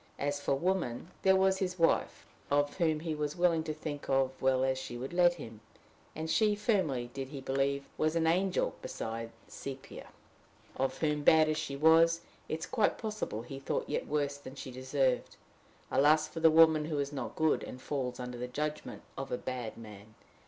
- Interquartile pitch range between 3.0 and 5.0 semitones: Yes, average, 3.6 semitones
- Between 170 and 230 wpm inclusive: Yes, average, 195 wpm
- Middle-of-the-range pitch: Yes, medium, 145 Hz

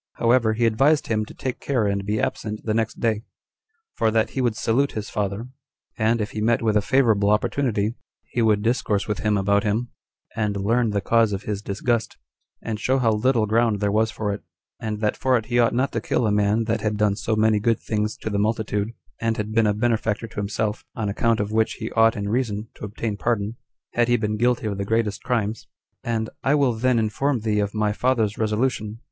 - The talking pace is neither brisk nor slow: No, fast, 225 wpm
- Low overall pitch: Yes, low, 110 Hz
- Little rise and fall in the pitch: Yes, narrow, 1.9 semitones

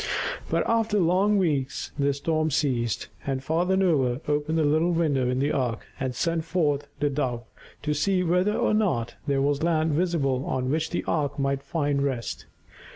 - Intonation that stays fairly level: No, average, 3.8 semitones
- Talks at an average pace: Yes, average, 175 wpm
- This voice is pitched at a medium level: Yes, medium, 150 Hz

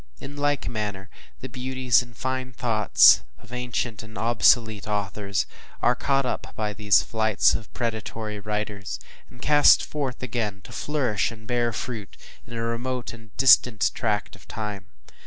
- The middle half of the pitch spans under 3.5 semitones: Yes, average, 2.9 semitones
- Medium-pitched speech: No, low, 115 Hz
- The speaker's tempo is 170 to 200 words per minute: No, average, 155 wpm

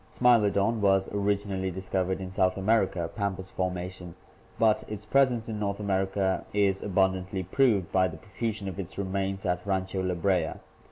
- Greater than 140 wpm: Yes, average, 165 wpm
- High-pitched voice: No, very low, 95 Hz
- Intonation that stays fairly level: Yes, narrow, 1.6 semitones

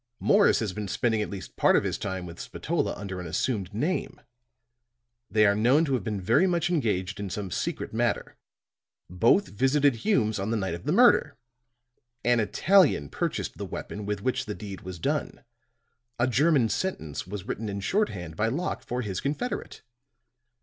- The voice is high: No, low, 105 Hz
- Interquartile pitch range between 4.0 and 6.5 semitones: Yes, wide, 5.6 semitones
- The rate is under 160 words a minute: No, average, 175 wpm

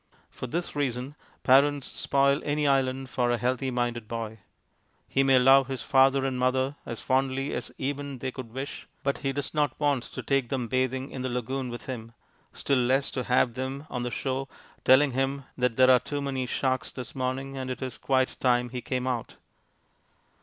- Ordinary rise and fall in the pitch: No, narrow, 1.4 semitones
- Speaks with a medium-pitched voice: No, low, 130 Hz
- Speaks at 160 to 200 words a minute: Yes, average, 195 wpm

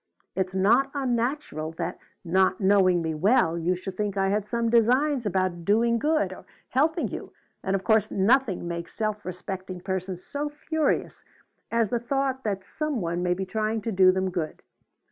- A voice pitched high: Yes, high, 200 Hz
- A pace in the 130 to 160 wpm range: No, average, 175 wpm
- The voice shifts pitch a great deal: No, average, 4.5 semitones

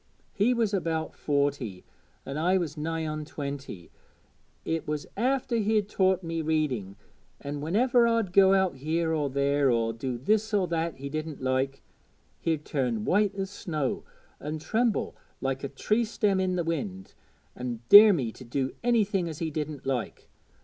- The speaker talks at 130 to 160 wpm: No, average, 170 wpm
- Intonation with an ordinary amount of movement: No, wide, 5.9 semitones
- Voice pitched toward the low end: No, medium, 160 Hz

